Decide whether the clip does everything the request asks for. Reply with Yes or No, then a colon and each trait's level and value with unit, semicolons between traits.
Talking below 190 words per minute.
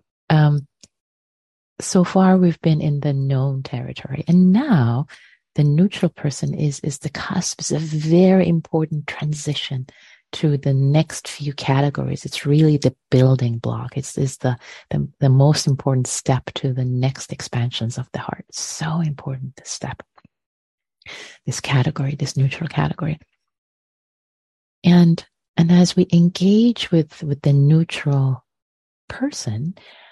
Yes: slow, 135 wpm